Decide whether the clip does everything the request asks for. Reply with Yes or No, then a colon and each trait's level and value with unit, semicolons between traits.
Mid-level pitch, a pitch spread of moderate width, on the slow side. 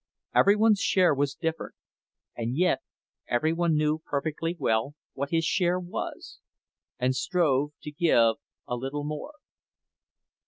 Yes: medium, 155 Hz; average, 4.2 semitones; slow, 125 wpm